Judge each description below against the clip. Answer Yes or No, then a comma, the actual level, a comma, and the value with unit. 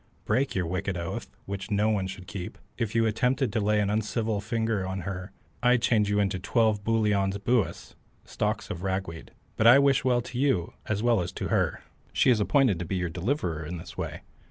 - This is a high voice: No, low, 105 Hz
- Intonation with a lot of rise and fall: No, average, 3.5 semitones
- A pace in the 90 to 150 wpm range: No, fast, 205 wpm